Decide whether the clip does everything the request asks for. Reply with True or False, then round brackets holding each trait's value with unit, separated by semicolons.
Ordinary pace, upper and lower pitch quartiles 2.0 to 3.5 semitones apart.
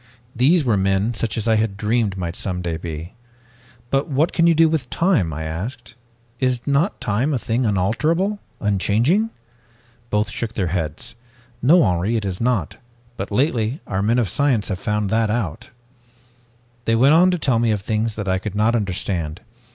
False (180 wpm; 5.1 semitones)